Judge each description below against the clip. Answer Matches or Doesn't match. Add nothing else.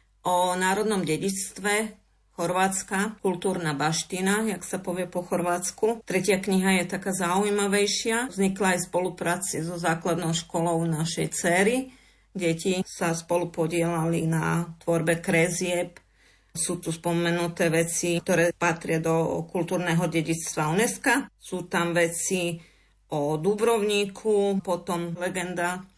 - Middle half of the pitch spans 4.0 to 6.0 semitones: Doesn't match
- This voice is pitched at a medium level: Matches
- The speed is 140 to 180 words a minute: Doesn't match